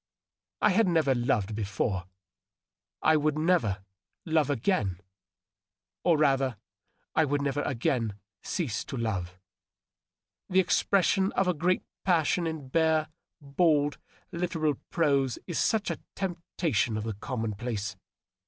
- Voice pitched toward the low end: No, medium, 145 Hz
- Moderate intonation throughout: No, wide, 7.1 semitones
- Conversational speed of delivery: No, slow, 125 wpm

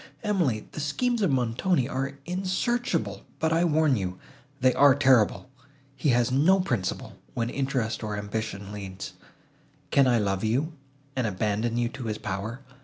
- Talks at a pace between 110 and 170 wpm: Yes, average, 155 wpm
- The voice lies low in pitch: Yes, low, 130 Hz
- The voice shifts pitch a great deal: Yes, wide, 5.8 semitones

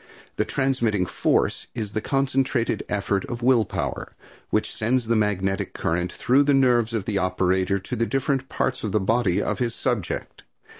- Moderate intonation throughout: Yes, average, 4.7 semitones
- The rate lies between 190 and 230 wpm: No, average, 170 wpm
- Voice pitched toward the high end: No, low, 115 Hz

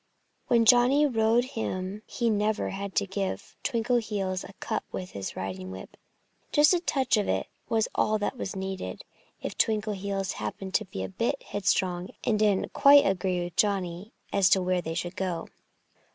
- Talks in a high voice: Yes, high, 200 Hz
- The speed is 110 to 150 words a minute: No, average, 170 wpm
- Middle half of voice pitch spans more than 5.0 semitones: No, average, 3.3 semitones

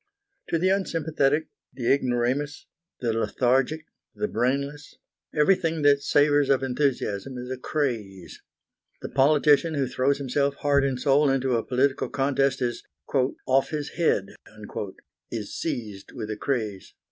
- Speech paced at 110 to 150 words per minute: Yes, slow, 135 wpm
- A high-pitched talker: No, low, 135 Hz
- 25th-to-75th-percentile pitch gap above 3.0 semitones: No, average, 2.7 semitones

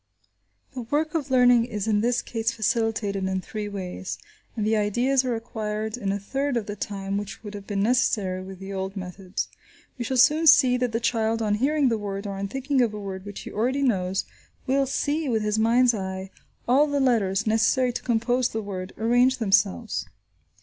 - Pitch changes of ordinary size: Yes, average, 3.9 semitones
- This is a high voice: Yes, high, 220 Hz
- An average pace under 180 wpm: No, average, 200 wpm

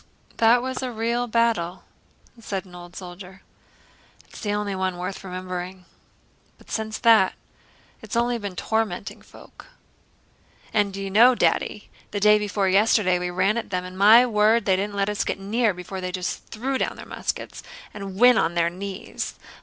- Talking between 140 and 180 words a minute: Yes, average, 175 wpm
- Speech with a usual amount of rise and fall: Yes, average, 3.3 semitones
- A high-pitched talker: Yes, high, 200 Hz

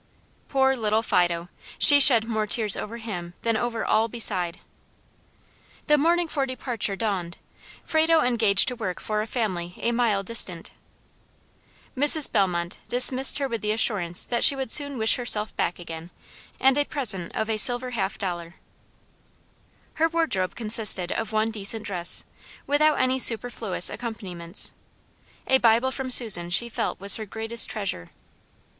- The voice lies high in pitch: Yes, high, 225 Hz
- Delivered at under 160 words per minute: Yes, average, 150 wpm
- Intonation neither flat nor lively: Yes, average, 4.6 semitones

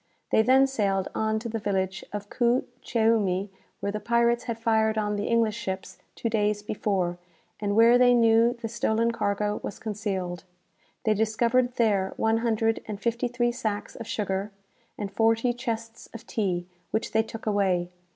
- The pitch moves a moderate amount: No, narrow, 2.3 semitones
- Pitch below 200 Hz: No, high, 220 Hz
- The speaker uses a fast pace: No, average, 170 wpm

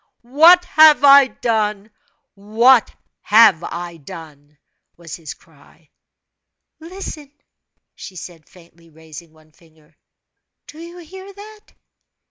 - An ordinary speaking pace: No, slow, 105 wpm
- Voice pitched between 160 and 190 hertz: No, high, 210 Hz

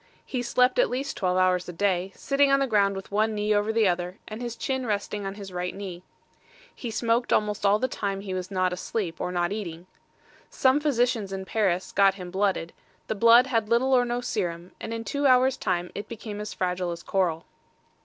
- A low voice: No, high, 205 Hz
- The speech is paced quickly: Yes, fast, 215 wpm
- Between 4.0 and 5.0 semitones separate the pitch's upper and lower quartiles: Yes, average, 4.3 semitones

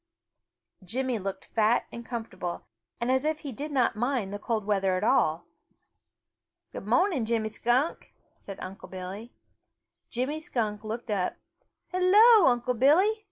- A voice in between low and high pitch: No, high, 235 Hz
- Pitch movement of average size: Yes, average, 4.5 semitones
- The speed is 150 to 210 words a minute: No, average, 140 wpm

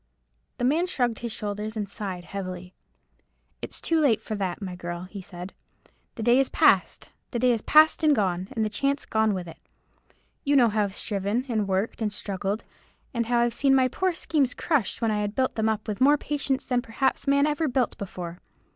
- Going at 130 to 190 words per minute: No, average, 200 wpm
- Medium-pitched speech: No, high, 220 Hz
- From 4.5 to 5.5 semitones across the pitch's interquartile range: Yes, average, 5.0 semitones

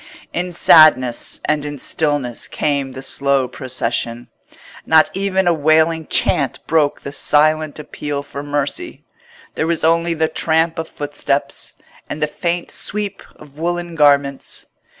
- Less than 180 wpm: Yes, slow, 135 wpm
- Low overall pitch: No, medium, 150 Hz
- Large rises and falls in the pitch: No, narrow, 2.5 semitones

